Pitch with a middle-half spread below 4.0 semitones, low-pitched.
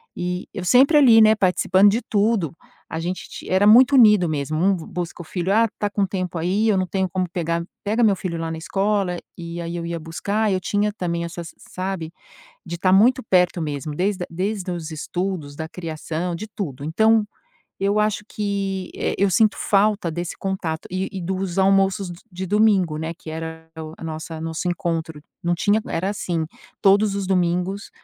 No: average, 3.3 semitones; medium, 185 Hz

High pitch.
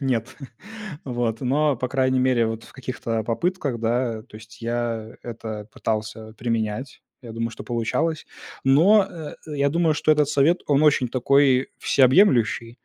No: low, 125 Hz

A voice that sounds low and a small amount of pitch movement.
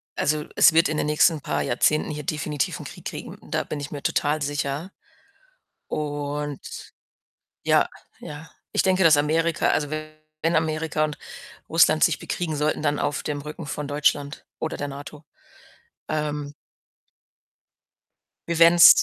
No: medium, 150 Hz; narrow, 1.4 semitones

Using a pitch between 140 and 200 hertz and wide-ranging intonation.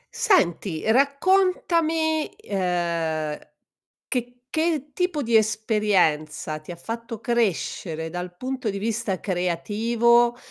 No: high, 220 Hz; wide, 7.3 semitones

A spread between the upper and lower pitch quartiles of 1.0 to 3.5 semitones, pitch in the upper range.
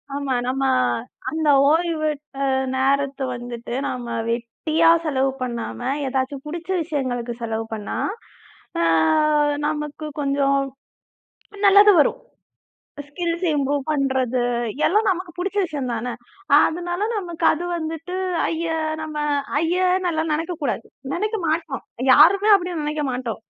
No: average, 4.5 semitones; very high, 300 Hz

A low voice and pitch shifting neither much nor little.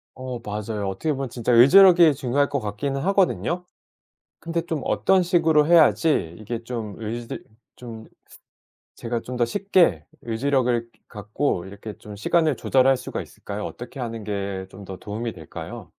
No: low, 120 Hz; wide, 6.0 semitones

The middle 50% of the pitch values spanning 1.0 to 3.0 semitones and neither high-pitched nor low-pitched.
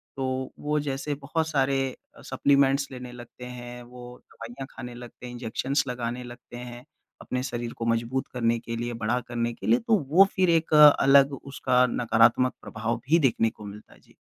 No: narrow, 2.5 semitones; low, 125 Hz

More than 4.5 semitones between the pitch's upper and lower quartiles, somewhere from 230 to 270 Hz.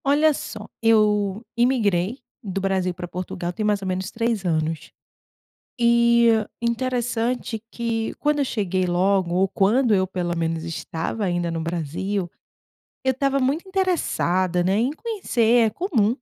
No: average, 4.9 semitones; high, 210 Hz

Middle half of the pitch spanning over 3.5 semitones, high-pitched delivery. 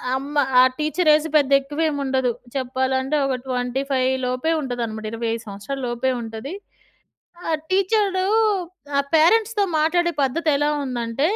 Yes: average, 4.1 semitones; very high, 270 Hz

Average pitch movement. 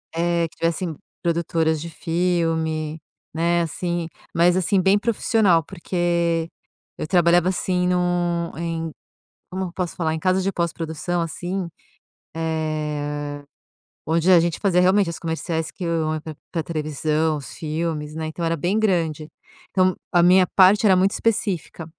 No: narrow, 2.0 semitones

